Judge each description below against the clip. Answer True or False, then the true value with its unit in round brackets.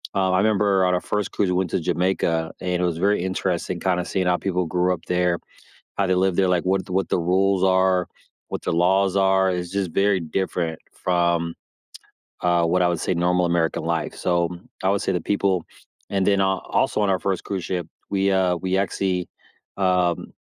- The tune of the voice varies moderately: False (1.6 semitones)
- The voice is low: True (90 Hz)